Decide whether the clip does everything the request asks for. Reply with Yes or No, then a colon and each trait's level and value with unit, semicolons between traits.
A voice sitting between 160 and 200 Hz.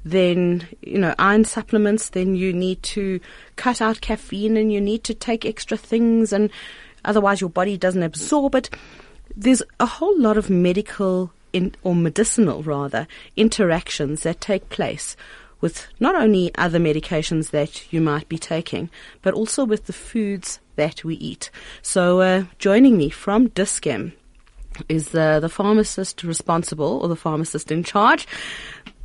Yes: medium, 185 Hz